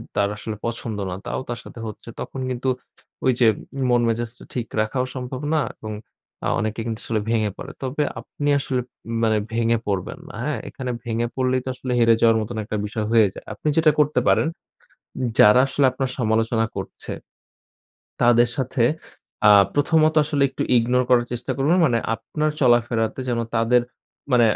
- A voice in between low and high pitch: No, low, 120 Hz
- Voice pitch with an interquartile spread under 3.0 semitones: Yes, narrow, 2.5 semitones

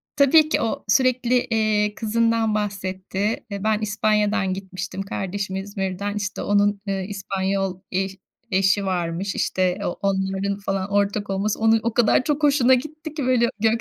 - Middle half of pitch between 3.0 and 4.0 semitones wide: No, narrow, 2.6 semitones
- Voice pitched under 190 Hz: No, high, 205 Hz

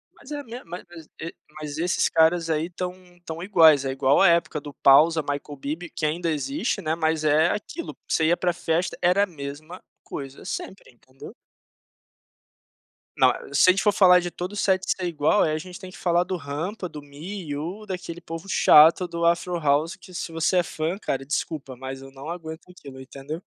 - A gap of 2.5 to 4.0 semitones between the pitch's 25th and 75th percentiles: Yes, average, 3.4 semitones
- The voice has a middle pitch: Yes, medium, 165 Hz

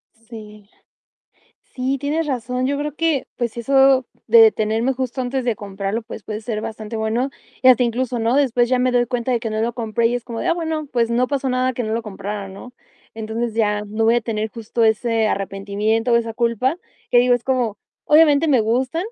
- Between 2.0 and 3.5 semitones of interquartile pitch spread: Yes, average, 2.7 semitones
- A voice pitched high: Yes, high, 235 Hz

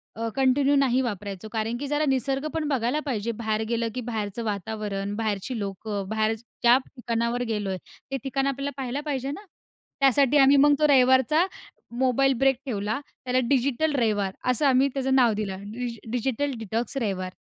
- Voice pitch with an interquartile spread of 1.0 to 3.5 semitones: No, average, 3.9 semitones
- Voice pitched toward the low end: No, high, 245 Hz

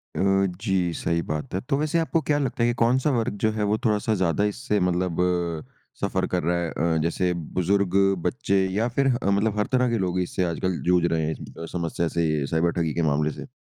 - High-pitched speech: No, very low, 90 Hz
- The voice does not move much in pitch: No, average, 4.7 semitones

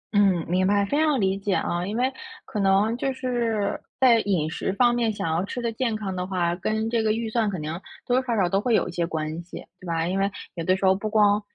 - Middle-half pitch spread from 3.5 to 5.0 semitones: Yes, average, 3.8 semitones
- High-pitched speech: Yes, high, 200 Hz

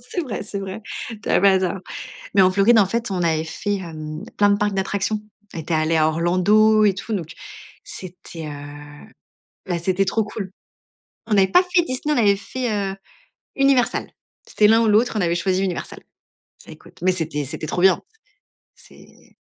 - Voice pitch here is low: No, high, 195 Hz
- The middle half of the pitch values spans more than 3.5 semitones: Yes, average, 3.9 semitones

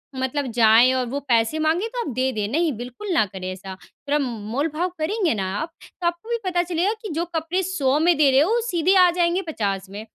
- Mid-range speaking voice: No, very high, 300 Hz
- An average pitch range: No, wide, 7.0 semitones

